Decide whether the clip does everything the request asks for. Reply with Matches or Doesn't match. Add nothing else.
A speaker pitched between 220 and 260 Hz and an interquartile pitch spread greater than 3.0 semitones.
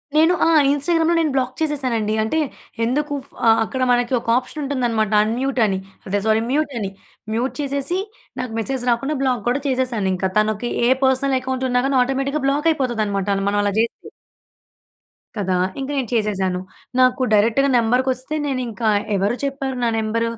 Matches